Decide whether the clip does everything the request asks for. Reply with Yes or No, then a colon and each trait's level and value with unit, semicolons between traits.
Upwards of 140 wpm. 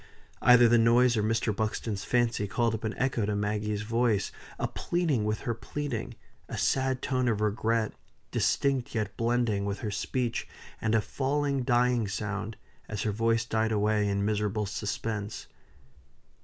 Yes: average, 155 wpm